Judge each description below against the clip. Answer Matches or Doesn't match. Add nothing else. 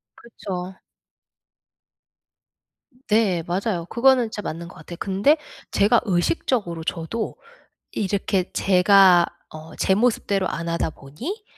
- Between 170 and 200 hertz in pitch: Matches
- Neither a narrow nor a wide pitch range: Matches